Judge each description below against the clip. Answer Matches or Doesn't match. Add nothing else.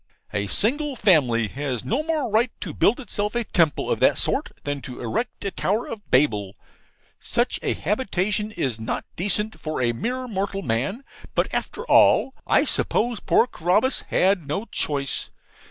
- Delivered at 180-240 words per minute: Doesn't match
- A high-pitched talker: Matches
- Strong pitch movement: Matches